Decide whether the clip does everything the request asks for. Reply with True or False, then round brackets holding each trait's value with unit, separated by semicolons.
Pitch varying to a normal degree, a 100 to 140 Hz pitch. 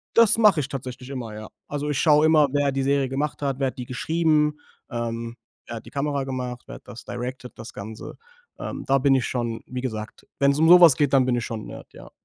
True (3.2 semitones; 135 Hz)